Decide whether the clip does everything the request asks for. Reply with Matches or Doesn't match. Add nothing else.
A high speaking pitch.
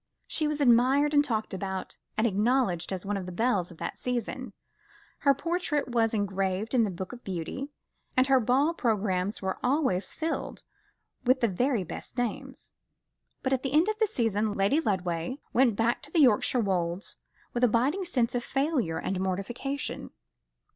Matches